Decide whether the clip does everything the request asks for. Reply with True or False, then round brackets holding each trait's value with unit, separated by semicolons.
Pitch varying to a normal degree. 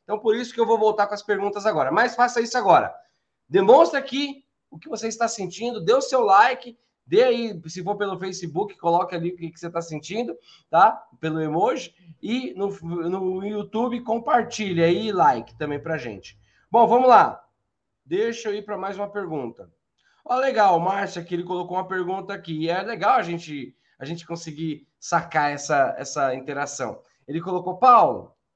False (5.7 semitones)